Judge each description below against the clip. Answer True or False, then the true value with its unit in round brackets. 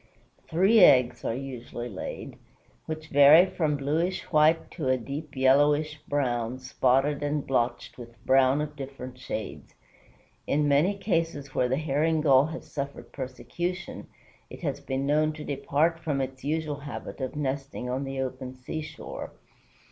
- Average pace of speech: True (150 wpm)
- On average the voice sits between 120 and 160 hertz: True (140 Hz)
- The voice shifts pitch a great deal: False (2.8 semitones)